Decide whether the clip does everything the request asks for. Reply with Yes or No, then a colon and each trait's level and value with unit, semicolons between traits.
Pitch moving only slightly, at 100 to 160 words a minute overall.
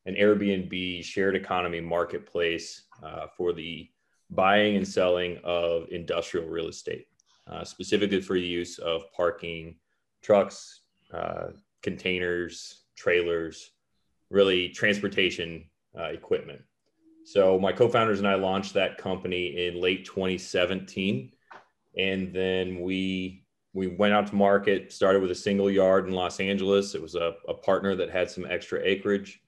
Yes: narrow, 2.2 semitones; average, 140 wpm